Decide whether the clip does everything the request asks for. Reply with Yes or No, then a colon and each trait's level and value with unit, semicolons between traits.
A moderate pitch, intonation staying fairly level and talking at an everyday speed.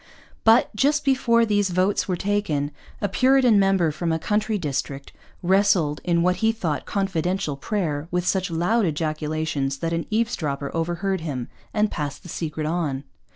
No: medium, 175 Hz; average, 4.9 semitones; average, 155 wpm